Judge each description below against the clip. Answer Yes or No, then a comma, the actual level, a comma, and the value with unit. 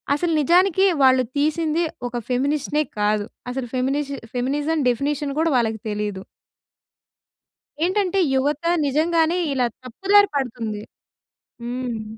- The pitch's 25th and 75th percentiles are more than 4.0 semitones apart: Yes, average, 4.7 semitones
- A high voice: Yes, very high, 280 Hz